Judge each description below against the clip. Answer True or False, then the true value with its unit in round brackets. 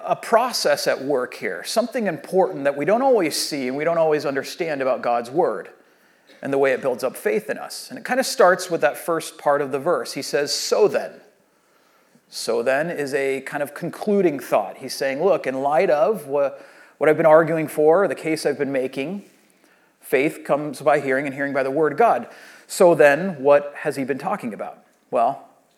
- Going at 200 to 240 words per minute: True (205 wpm)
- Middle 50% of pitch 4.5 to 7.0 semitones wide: True (5.6 semitones)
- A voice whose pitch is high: False (155 Hz)